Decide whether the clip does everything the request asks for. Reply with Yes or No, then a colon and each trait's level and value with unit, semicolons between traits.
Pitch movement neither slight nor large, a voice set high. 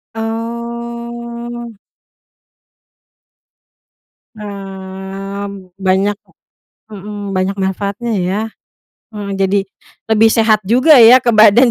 Yes: average, 3.2 semitones; high, 210 Hz